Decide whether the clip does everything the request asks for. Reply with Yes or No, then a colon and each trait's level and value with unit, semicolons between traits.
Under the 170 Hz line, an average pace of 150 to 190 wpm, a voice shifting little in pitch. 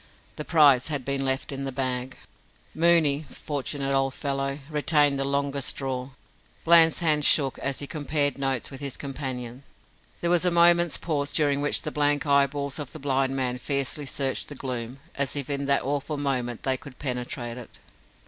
Yes: medium, 140 Hz; average, 175 wpm; narrow, 1.7 semitones